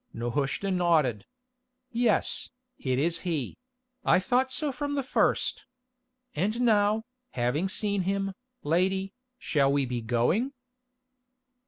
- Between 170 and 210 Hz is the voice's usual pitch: Yes, medium, 185 Hz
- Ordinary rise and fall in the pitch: No, wide, 7.6 semitones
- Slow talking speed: Yes, slow, 115 wpm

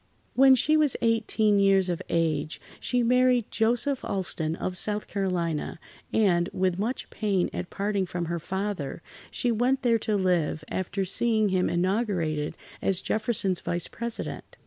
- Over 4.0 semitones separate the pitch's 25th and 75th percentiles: Yes, average, 4.6 semitones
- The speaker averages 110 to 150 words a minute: Yes, average, 145 wpm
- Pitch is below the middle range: No, high, 195 Hz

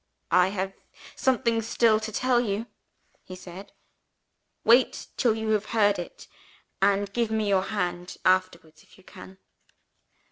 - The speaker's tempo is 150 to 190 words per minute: No, average, 140 wpm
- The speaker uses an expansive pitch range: No, average, 3.1 semitones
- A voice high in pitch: Yes, high, 205 Hz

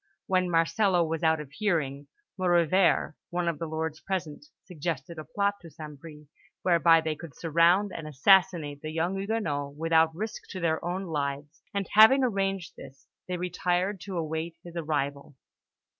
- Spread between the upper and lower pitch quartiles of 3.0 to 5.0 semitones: Yes, average, 3.3 semitones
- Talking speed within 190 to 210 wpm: No, average, 160 wpm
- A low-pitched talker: No, medium, 165 Hz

